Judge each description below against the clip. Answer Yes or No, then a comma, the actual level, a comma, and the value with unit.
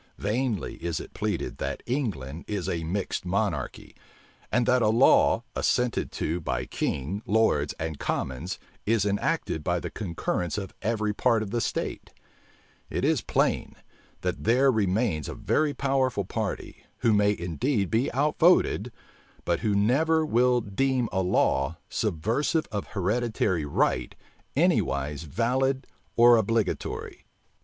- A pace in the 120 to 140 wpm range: Yes, slow, 135 wpm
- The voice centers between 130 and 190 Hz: No, low, 105 Hz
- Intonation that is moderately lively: No, wide, 5.8 semitones